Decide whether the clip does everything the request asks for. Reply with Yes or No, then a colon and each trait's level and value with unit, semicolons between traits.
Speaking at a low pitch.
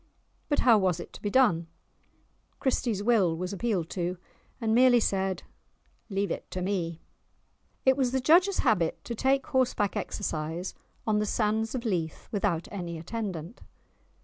No: high, 205 Hz